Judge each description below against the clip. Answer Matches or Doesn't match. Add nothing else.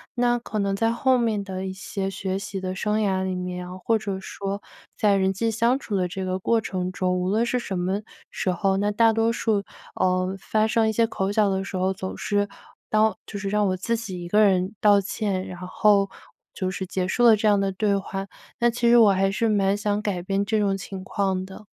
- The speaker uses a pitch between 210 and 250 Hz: Doesn't match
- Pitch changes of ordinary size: Doesn't match